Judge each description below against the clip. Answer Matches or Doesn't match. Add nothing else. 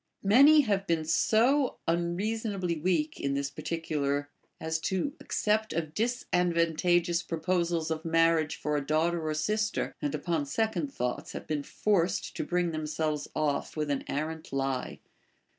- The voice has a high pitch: Doesn't match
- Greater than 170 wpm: Doesn't match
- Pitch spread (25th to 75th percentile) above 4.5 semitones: Doesn't match